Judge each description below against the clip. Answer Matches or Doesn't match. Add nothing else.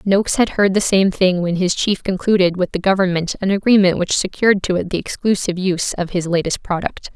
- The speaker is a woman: Matches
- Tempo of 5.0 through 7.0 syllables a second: Matches